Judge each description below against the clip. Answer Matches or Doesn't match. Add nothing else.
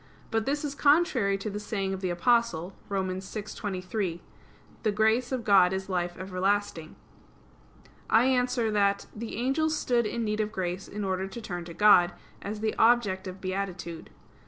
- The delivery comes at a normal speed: Matches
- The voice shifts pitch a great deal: Doesn't match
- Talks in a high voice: Matches